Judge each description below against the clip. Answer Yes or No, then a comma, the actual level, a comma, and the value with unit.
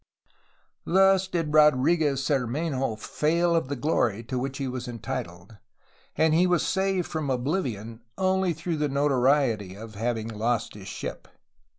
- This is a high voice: No, low, 135 Hz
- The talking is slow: No, average, 145 wpm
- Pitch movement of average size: No, wide, 5.9 semitones